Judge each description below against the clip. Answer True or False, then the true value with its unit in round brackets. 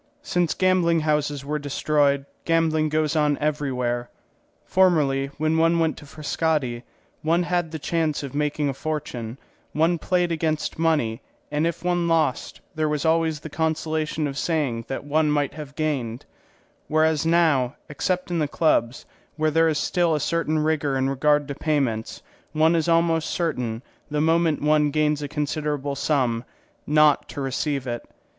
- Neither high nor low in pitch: True (150 Hz)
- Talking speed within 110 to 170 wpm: True (160 wpm)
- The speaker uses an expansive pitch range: False (2.4 semitones)